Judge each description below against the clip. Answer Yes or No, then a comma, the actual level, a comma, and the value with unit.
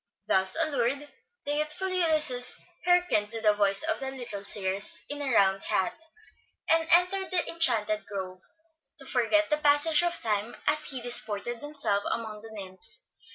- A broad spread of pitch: Yes, wide, 6.8 semitones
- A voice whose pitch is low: No, very high, 250 Hz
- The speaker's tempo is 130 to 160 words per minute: Yes, average, 155 wpm